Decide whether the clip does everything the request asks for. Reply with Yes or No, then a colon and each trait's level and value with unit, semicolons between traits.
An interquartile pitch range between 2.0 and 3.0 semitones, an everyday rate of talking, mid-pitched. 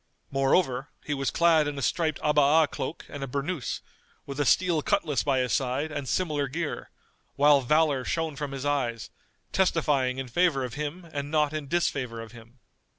Yes: average, 2.7 semitones; average, 180 wpm; medium, 145 Hz